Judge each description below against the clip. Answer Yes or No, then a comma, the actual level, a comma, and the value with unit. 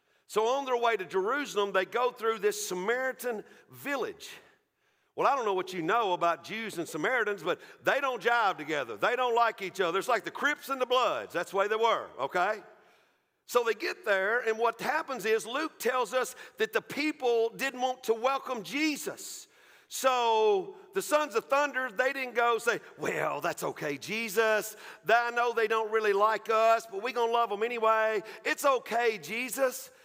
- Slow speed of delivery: No, average, 190 wpm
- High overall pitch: Yes, high, 235 Hz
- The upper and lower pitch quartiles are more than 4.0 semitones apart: No, average, 3.6 semitones